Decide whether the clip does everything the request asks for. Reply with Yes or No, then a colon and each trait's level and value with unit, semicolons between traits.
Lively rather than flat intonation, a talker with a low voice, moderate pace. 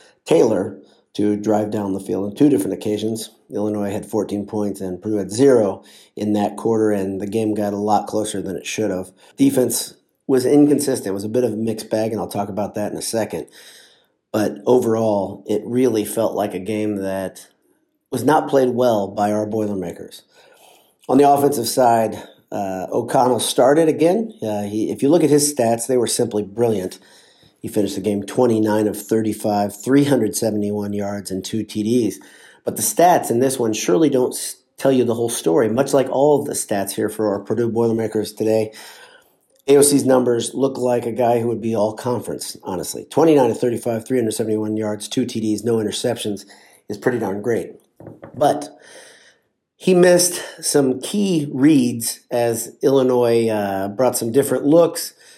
No: average, 3.4 semitones; low, 110 Hz; average, 175 wpm